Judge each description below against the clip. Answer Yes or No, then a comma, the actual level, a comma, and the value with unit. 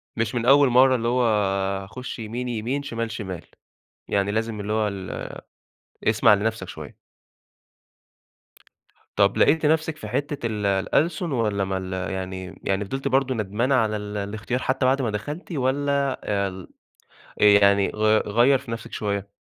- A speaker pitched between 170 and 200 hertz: No, low, 115 Hz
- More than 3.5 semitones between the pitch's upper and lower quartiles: Yes, average, 4.3 semitones